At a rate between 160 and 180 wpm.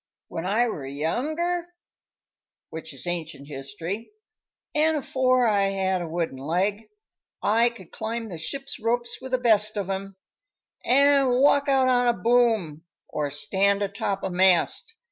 No: average, 145 wpm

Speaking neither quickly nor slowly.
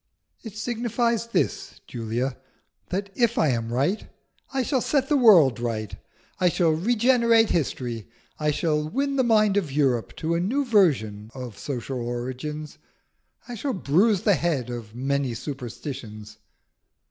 Yes: average, 145 wpm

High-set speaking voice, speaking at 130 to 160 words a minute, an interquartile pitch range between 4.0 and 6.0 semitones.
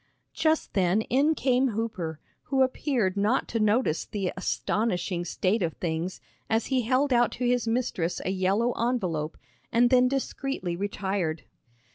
Yes: high, 220 Hz; average, 145 wpm; wide, 5.4 semitones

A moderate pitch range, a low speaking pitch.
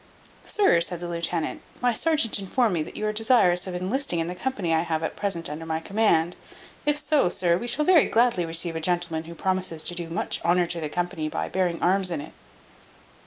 No: average, 4.2 semitones; medium, 175 Hz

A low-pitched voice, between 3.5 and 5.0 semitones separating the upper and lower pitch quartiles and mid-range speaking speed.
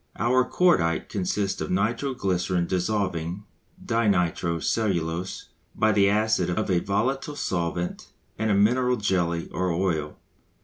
No: very low, 95 Hz; average, 3.9 semitones; slow, 130 wpm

